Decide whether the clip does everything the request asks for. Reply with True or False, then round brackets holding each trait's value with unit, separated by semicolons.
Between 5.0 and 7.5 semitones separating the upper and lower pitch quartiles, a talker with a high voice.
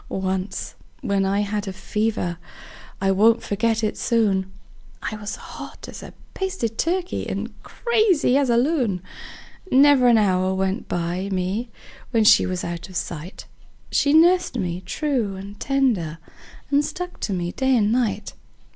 True (5.4 semitones; 210 Hz)